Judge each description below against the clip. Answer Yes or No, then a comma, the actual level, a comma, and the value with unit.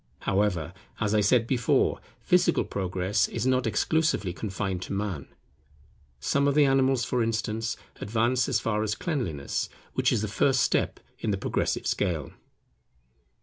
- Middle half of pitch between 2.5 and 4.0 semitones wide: No, average, 4.6 semitones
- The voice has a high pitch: No, low, 110 Hz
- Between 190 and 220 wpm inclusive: No, average, 145 wpm